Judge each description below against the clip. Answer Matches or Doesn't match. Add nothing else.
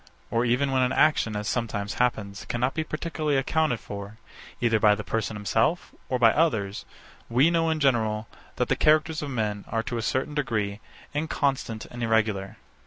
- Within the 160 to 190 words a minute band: Matches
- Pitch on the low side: Matches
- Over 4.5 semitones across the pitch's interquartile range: Matches